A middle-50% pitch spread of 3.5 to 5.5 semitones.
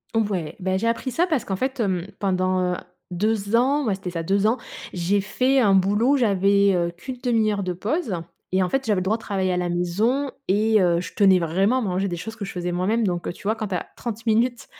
Yes: average, 3.8 semitones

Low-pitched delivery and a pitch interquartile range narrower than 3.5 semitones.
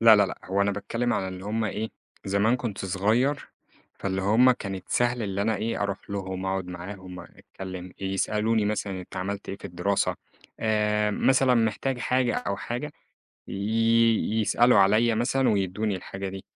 Yes: low, 105 Hz; average, 3.0 semitones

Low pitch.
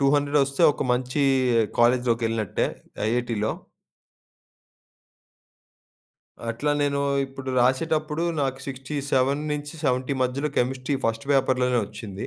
Yes: low, 130 Hz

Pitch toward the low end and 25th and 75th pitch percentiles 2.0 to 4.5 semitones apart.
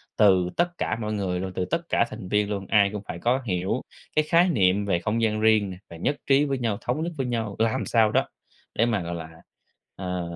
Yes: low, 105 Hz; average, 4.2 semitones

